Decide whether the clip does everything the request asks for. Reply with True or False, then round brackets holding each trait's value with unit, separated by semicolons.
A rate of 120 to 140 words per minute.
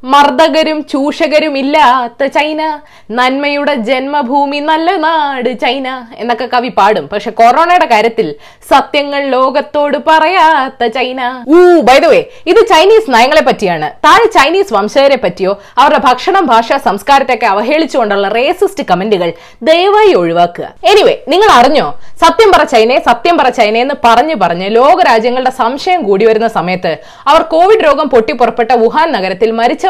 True (125 wpm)